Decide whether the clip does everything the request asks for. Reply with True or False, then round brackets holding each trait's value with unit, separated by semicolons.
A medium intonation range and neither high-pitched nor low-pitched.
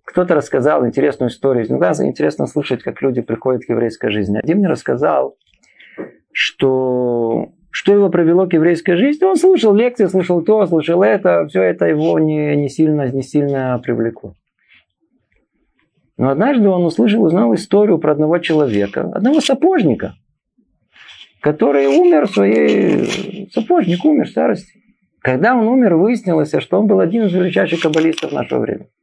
False (8.1 semitones; 165 Hz)